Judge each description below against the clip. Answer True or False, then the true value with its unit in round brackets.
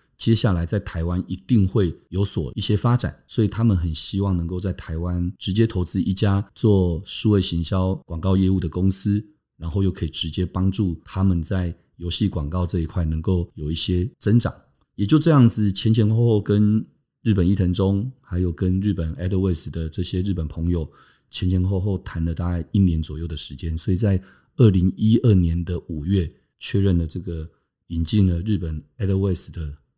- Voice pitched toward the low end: True (95 Hz)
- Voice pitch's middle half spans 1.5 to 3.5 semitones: True (3.2 semitones)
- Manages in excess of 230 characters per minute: True (300 characters per minute)